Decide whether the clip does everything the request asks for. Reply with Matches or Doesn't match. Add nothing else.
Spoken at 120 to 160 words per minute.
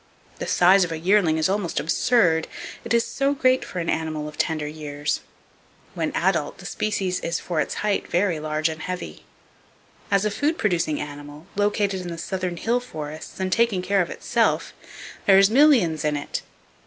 Doesn't match